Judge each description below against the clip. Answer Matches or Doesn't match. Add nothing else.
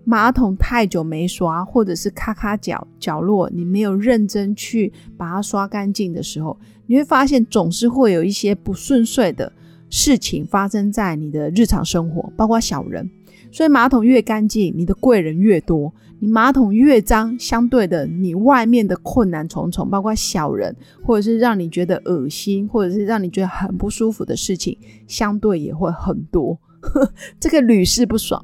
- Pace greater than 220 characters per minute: Matches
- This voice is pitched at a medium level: Doesn't match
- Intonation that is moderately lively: Matches